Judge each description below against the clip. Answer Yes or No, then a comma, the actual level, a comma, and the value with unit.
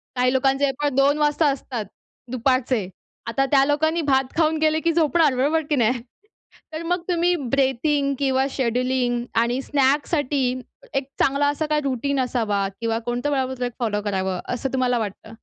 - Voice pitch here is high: Yes, very high, 270 Hz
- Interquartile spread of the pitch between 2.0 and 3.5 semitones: Yes, average, 2.9 semitones